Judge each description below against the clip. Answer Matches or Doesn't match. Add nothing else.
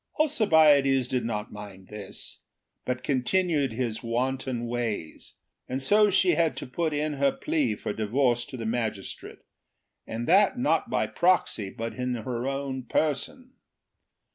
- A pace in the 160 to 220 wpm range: Doesn't match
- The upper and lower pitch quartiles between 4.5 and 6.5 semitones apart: Matches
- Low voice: Matches